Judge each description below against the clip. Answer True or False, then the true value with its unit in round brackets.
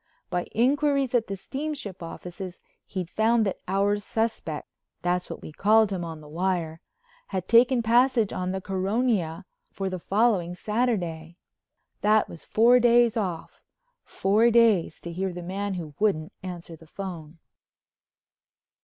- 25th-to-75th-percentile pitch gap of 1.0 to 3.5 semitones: False (4.8 semitones)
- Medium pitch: False (195 Hz)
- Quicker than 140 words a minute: False (135 wpm)